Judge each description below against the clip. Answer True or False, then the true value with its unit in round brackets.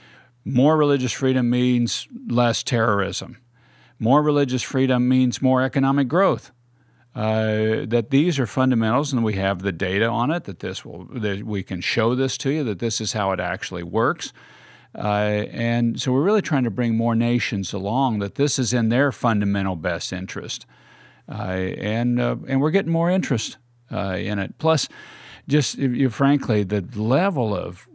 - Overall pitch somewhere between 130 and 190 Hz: False (120 Hz)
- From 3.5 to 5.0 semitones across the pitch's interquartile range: True (4.2 semitones)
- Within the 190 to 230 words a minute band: False (170 wpm)